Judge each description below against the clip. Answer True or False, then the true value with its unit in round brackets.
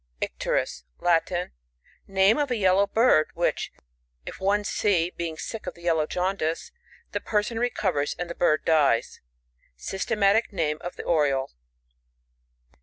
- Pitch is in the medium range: True (180 Hz)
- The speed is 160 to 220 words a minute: False (140 wpm)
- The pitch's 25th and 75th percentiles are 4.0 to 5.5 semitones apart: True (4.4 semitones)